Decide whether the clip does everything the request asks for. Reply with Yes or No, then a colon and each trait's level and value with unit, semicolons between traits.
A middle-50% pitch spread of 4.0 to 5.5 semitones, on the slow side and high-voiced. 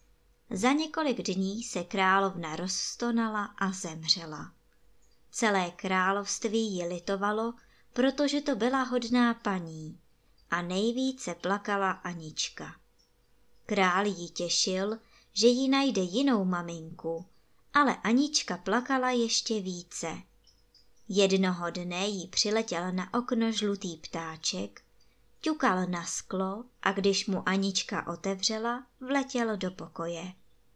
Yes: average, 4.8 semitones; slow, 105 wpm; high, 195 Hz